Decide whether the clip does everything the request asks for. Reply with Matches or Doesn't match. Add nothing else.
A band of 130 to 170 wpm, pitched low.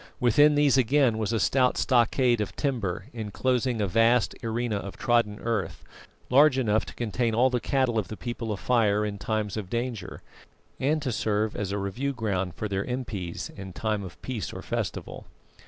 Doesn't match